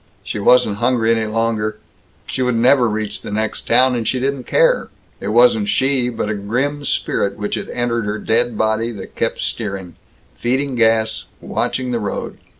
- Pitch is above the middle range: No, low, 115 Hz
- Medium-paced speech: Yes, average, 175 wpm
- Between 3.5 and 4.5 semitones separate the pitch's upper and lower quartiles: No, narrow, 2.6 semitones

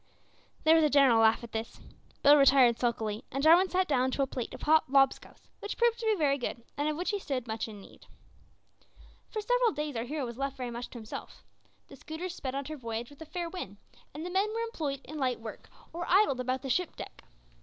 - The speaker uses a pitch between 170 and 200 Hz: No, very high, 275 Hz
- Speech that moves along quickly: Yes, fast, 235 wpm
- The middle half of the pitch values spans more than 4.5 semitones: Yes, wide, 5.4 semitones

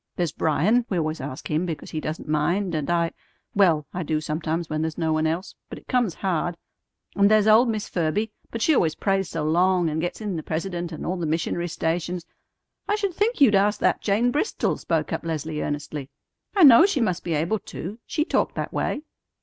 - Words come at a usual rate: No, fast, 215 wpm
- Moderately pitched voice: Yes, medium, 175 Hz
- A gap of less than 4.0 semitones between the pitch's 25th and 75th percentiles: No, average, 4.8 semitones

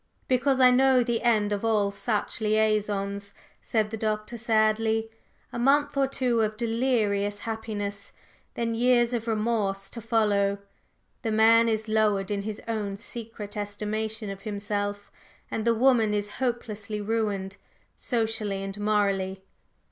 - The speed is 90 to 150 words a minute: Yes, average, 140 wpm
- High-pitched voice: Yes, high, 215 Hz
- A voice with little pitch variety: Yes, narrow, 2.1 semitones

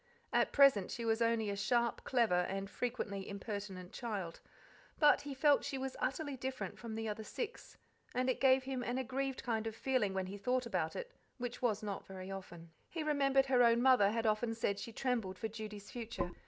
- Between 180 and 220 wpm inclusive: Yes, average, 200 wpm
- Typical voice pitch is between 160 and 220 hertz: No, high, 230 Hz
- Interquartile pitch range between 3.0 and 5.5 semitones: Yes, average, 4.4 semitones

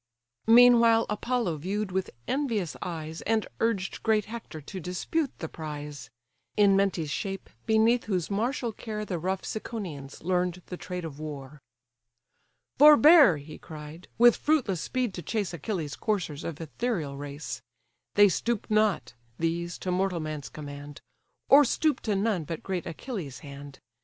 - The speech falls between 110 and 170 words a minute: Yes, average, 145 wpm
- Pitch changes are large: Yes, wide, 6.1 semitones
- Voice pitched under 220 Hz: Yes, medium, 185 Hz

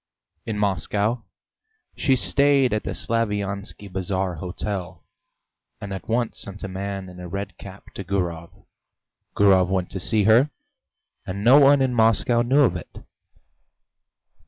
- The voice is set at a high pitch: No, low, 100 Hz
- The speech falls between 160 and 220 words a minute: No, average, 140 wpm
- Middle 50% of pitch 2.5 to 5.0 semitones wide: Yes, average, 3.5 semitones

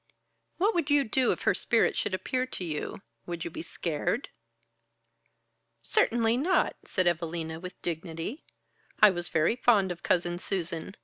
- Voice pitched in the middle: Yes, medium, 180 Hz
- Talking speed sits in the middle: Yes, average, 150 wpm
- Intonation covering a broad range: Yes, wide, 6.2 semitones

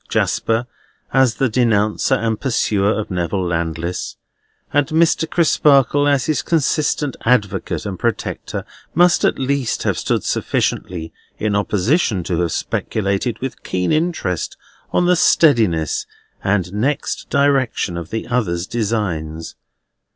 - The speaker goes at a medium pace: No, slow, 125 wpm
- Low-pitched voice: Yes, low, 110 Hz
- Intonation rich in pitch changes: Yes, wide, 7.0 semitones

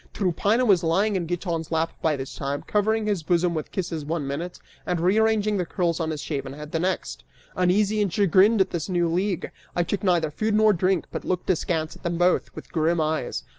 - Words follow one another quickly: Yes, fast, 210 wpm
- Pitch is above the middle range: No, medium, 175 Hz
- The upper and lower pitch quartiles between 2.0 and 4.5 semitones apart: Yes, average, 3.6 semitones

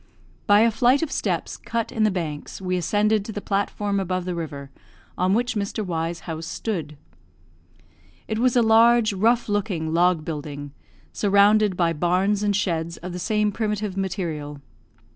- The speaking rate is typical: Yes, average, 165 wpm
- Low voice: No, high, 195 Hz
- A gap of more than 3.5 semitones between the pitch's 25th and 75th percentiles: Yes, average, 4.2 semitones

